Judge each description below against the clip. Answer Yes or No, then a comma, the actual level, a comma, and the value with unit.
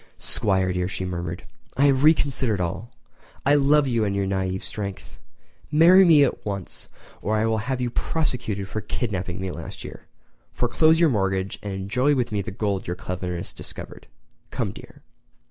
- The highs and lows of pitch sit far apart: Yes, wide, 5.9 semitones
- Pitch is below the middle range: Yes, low, 105 Hz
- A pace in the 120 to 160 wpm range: No, average, 170 wpm